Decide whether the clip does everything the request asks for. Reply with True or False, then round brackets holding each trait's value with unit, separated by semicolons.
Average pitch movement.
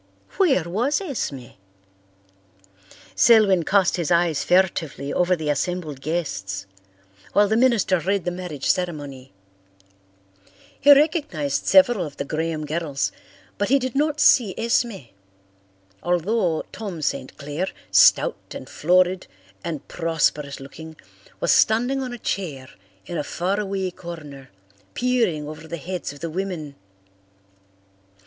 False (6.1 semitones)